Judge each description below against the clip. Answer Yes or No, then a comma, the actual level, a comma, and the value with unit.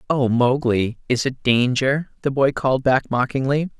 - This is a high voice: No, low, 130 Hz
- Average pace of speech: Yes, average, 160 wpm